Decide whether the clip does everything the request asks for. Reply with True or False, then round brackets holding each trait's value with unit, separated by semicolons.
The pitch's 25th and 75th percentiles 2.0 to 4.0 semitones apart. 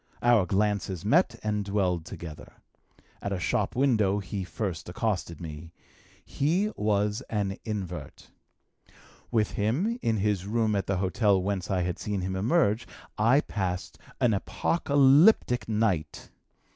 True (3.5 semitones)